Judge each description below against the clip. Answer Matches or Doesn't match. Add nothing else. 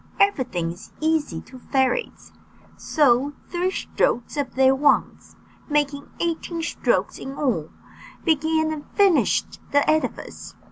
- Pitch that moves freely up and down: Doesn't match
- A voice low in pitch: Doesn't match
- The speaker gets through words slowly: Matches